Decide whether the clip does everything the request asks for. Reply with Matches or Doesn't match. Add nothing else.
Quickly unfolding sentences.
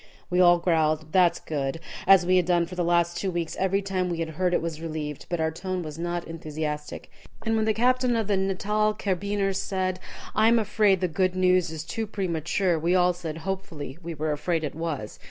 Matches